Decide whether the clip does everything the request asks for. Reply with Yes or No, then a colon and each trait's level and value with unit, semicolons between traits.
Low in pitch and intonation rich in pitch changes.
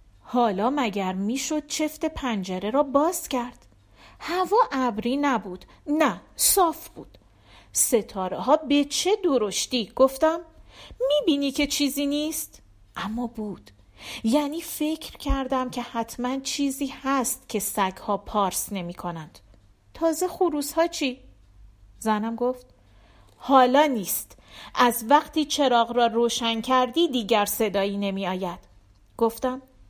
No: high, 245 Hz; wide, 6.6 semitones